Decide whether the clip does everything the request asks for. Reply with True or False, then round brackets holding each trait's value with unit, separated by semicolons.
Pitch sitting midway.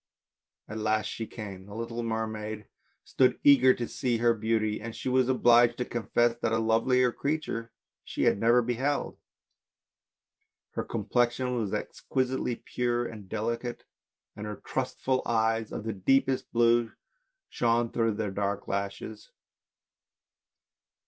False (115 Hz)